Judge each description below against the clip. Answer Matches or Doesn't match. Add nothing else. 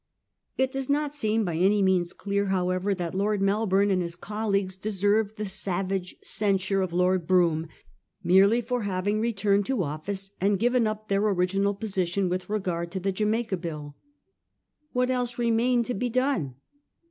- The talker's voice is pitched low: Doesn't match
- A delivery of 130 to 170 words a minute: Matches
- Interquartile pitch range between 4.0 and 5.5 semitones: Doesn't match